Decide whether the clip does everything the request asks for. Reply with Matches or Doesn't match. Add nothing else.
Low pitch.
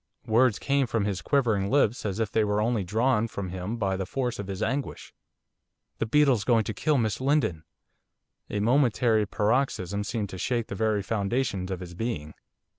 Matches